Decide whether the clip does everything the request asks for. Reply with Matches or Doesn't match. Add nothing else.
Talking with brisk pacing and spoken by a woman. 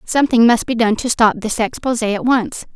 Matches